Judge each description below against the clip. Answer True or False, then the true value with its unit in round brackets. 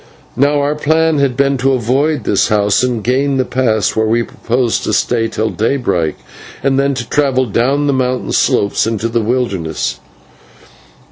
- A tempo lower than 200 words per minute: True (165 wpm)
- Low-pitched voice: True (125 Hz)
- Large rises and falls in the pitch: False (3.7 semitones)